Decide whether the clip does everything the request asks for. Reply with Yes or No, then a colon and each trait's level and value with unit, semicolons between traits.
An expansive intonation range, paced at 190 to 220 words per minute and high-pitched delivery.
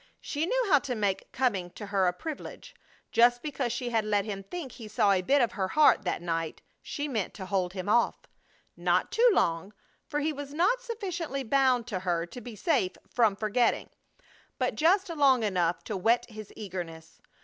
Yes: wide, 6.9 semitones; average, 195 wpm; high, 230 Hz